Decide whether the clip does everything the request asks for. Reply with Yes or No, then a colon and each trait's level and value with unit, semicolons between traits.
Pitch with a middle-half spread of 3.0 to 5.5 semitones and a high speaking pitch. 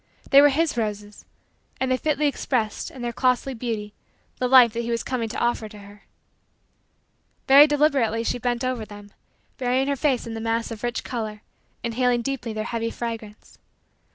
No: narrow, 2.6 semitones; high, 235 Hz